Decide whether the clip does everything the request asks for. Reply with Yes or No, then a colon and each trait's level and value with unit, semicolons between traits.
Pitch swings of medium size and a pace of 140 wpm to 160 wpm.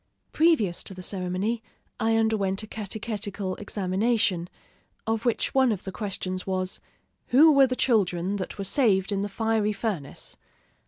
Yes: average, 3.1 semitones; average, 150 wpm